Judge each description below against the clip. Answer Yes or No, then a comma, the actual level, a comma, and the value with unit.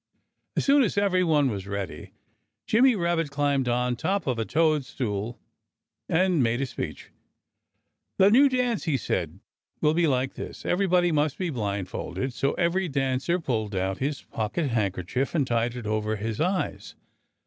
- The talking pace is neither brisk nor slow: Yes, average, 155 wpm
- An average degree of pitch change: No, wide, 7.3 semitones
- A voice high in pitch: No, low, 135 Hz